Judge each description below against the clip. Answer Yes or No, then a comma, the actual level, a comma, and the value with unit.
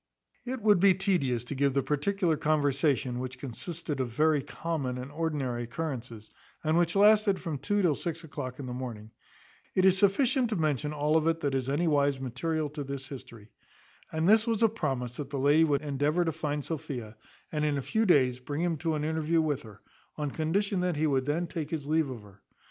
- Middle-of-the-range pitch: Yes, medium, 150 Hz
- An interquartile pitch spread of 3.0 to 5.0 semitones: Yes, average, 4.0 semitones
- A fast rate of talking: Yes, fast, 210 wpm